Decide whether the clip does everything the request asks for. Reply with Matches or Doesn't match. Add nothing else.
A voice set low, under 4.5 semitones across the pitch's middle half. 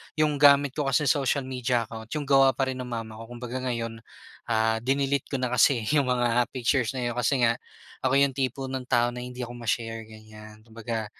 Matches